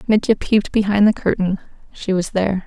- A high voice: Yes, high, 200 Hz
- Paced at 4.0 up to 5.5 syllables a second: No, 5.9 syllables/s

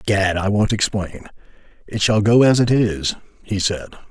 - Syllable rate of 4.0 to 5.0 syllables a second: Yes, 4.9 syllables/s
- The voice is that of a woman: No, male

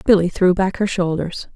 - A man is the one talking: No, female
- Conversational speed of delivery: Yes, average, 195 wpm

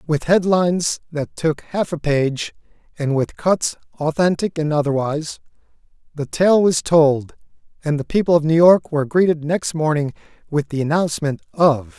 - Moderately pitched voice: Yes, medium, 155 Hz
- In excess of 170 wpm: No, average, 155 wpm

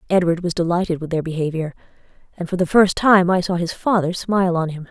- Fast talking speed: Yes, fast, 220 wpm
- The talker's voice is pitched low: No, medium, 175 Hz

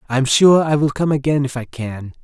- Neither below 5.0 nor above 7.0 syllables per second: Yes, 5.1 syllables/s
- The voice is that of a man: Yes, male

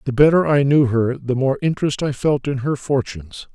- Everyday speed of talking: No, fast, 220 wpm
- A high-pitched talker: No, low, 135 Hz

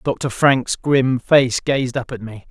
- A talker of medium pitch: No, low, 130 Hz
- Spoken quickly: No, average, 190 wpm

